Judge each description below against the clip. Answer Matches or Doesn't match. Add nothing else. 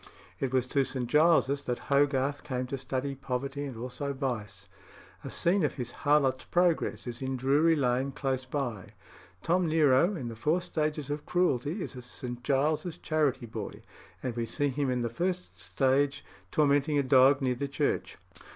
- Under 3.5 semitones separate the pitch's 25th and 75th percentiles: Matches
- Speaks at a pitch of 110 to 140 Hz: Matches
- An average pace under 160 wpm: Doesn't match